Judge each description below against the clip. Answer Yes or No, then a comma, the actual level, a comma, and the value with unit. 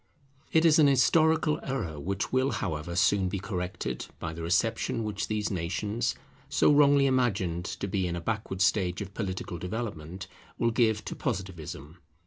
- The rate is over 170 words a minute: No, average, 160 wpm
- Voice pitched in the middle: No, low, 100 Hz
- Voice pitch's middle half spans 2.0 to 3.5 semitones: No, average, 5.2 semitones